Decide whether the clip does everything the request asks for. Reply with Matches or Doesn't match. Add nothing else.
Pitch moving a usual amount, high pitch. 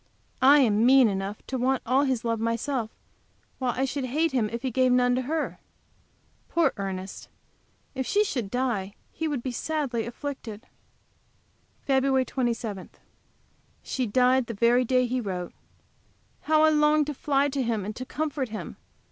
Matches